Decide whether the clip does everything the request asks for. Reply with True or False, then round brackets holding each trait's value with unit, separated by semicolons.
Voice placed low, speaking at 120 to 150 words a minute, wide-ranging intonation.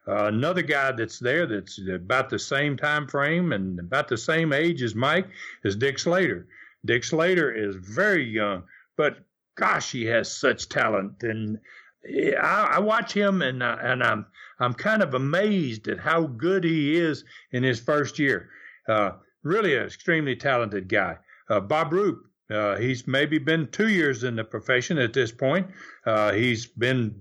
False (130 Hz; 170 wpm; 6.4 semitones)